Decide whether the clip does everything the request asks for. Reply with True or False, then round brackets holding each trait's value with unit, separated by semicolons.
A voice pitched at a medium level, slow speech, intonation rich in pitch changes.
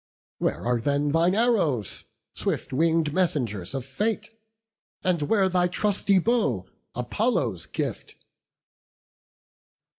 True (165 Hz; 100 wpm; 7.0 semitones)